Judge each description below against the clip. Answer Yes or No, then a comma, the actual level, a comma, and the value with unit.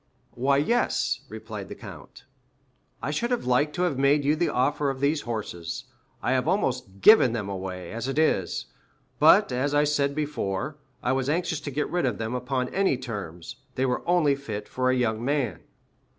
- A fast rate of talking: No, average, 190 wpm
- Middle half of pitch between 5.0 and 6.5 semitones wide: No, average, 4.2 semitones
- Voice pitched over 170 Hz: No, low, 130 Hz